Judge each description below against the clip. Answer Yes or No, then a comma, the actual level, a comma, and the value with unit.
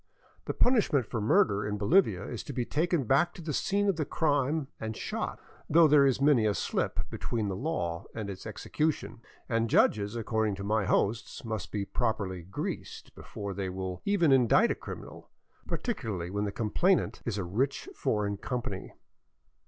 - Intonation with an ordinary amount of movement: No, wide, 6.2 semitones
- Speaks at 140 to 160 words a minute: No, average, 180 wpm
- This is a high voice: No, low, 115 Hz